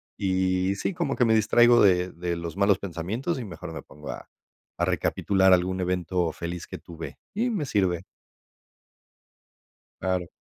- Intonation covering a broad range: No, average, 3.9 semitones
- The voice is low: Yes, very low, 95 Hz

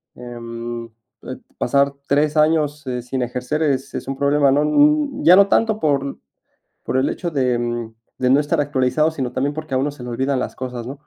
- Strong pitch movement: No, average, 3.2 semitones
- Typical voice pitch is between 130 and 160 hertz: Yes, medium, 140 Hz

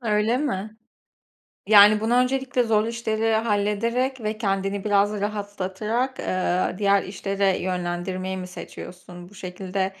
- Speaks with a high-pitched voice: Yes, high, 205 Hz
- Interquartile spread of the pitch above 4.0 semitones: No, average, 2.9 semitones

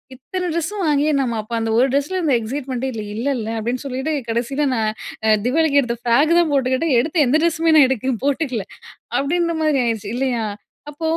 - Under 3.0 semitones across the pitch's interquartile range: No, average, 4.4 semitones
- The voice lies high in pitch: Yes, very high, 270 Hz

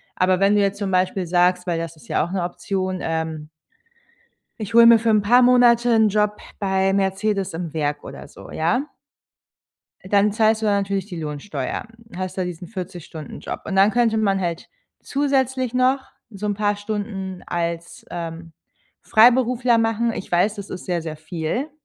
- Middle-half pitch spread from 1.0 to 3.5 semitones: No, average, 3.9 semitones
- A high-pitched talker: Yes, high, 195 Hz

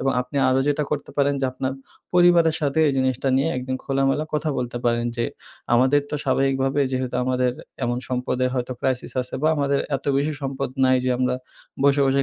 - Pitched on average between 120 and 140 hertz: Yes, low, 135 Hz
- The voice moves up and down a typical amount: No, narrow, 1.9 semitones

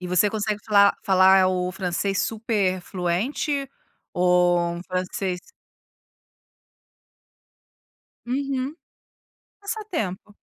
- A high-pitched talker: Yes, high, 195 Hz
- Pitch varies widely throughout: No, average, 3.7 semitones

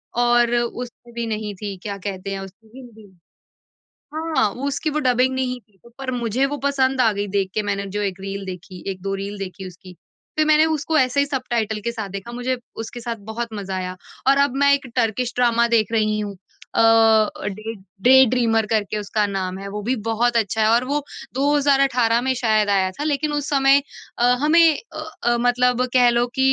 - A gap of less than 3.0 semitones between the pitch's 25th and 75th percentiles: No, average, 4.2 semitones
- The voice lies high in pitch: Yes, high, 235 Hz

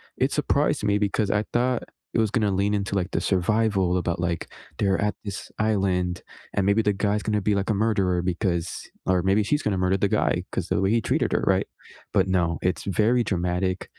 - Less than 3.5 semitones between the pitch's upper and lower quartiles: Yes, narrow, 2.4 semitones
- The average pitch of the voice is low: Yes, low, 100 Hz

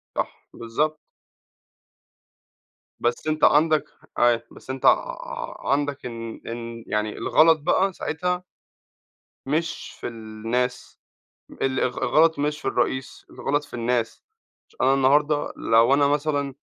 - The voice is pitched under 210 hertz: Yes, medium, 140 Hz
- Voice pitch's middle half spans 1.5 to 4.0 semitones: No, average, 4.4 semitones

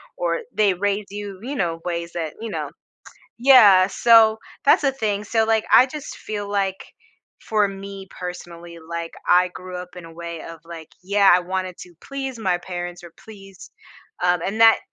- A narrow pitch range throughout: No, average, 3.5 semitones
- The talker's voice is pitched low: No, high, 190 Hz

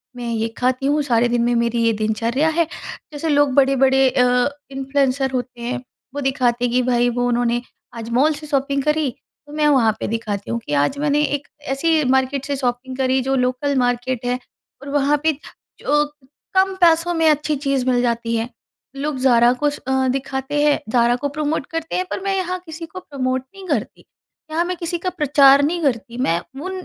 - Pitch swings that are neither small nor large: Yes, average, 3.3 semitones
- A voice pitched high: Yes, very high, 270 Hz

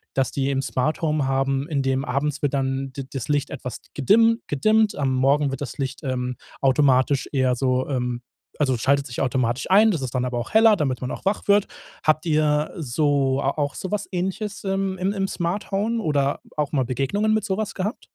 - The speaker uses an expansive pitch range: Yes, wide, 6.1 semitones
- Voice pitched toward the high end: No, medium, 140 Hz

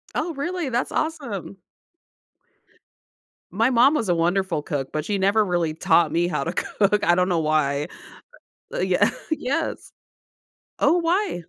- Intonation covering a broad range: Yes, wide, 8.8 semitones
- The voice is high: Yes, high, 195 Hz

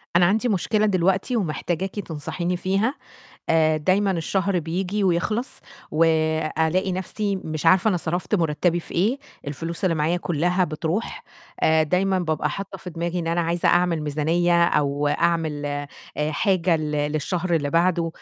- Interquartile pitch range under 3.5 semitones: Yes, average, 2.9 semitones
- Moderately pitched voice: Yes, medium, 170 Hz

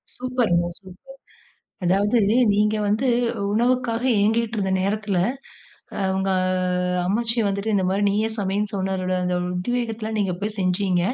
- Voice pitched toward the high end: Yes, high, 205 Hz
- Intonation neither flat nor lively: Yes, average, 3.1 semitones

